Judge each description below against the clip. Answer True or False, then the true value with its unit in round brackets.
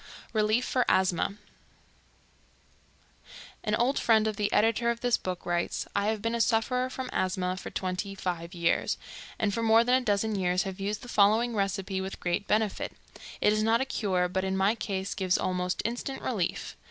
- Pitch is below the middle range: False (205 Hz)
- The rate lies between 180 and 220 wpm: True (185 wpm)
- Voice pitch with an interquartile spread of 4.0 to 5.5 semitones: False (3.3 semitones)